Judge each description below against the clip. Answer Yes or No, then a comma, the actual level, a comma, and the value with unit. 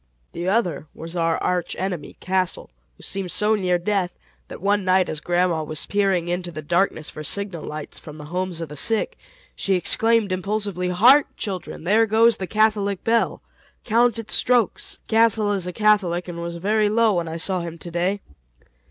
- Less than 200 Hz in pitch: Yes, medium, 185 Hz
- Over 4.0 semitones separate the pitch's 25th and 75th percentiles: No, average, 3.6 semitones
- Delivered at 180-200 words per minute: Yes, average, 185 wpm